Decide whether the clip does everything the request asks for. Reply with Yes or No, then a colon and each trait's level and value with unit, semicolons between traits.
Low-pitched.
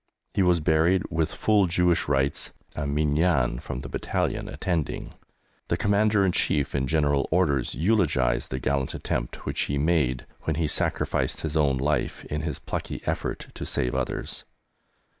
Yes: very low, 75 Hz